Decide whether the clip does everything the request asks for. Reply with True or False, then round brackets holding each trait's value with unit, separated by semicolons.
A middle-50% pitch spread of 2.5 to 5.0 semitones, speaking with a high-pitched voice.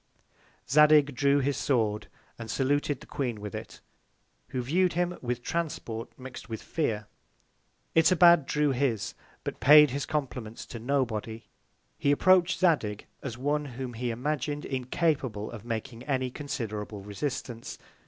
False (4.3 semitones; 130 Hz)